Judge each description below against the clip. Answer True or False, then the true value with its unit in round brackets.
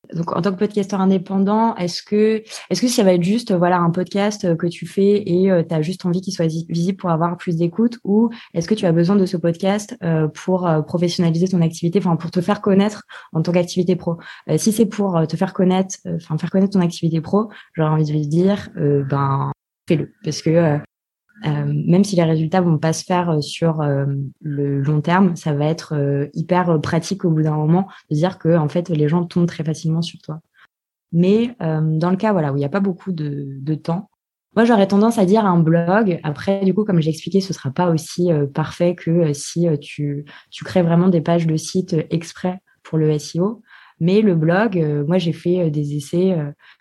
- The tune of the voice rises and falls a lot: False (3.2 semitones)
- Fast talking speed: True (230 wpm)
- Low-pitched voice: False (170 Hz)